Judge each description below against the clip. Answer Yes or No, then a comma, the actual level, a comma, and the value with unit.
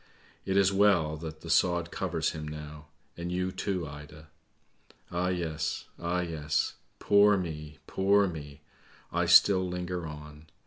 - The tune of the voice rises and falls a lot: No, average, 3.1 semitones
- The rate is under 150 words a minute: Yes, average, 140 wpm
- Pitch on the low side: Yes, very low, 85 Hz